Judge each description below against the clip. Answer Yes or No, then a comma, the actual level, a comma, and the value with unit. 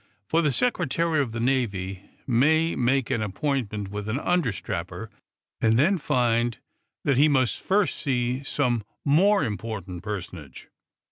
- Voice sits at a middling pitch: No, low, 120 Hz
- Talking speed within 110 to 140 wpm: Yes, slow, 135 wpm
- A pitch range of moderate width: No, wide, 5.7 semitones